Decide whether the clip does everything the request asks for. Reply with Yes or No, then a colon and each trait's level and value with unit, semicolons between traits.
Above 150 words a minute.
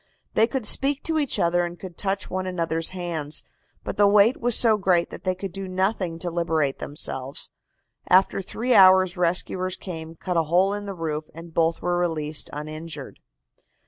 Yes: average, 180 wpm